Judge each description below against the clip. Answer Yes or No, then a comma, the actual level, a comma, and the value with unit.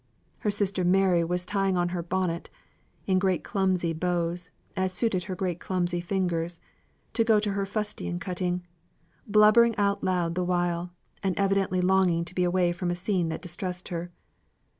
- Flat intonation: Yes, narrow, 1.8 semitones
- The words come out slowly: No, average, 165 wpm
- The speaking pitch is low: No, medium, 180 Hz